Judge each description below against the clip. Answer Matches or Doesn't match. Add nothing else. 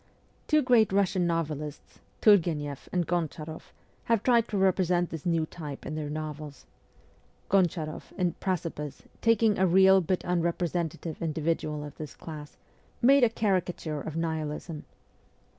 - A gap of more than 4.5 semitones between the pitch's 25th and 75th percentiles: Doesn't match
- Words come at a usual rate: Doesn't match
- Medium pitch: Matches